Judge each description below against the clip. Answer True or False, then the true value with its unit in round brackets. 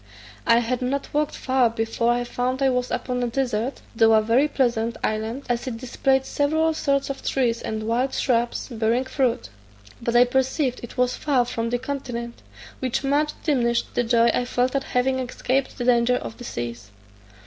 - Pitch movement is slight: True (2.1 semitones)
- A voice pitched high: True (250 Hz)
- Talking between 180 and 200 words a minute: True (185 wpm)